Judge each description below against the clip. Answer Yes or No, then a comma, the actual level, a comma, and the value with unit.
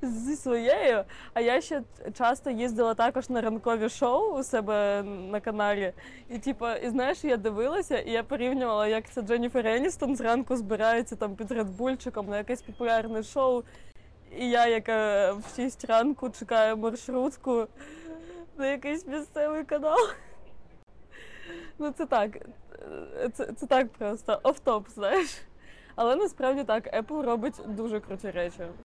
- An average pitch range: Yes, average, 3.7 semitones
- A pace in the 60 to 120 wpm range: No, average, 135 wpm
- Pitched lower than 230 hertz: No, high, 240 Hz